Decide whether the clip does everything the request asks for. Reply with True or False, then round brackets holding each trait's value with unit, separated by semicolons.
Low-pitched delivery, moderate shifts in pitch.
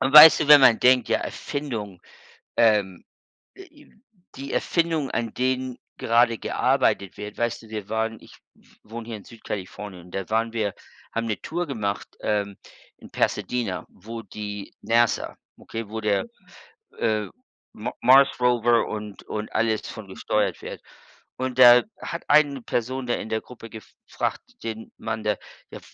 True (115 Hz; 3.0 semitones)